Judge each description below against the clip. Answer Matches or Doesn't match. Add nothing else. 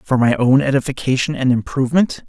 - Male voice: Matches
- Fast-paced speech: Doesn't match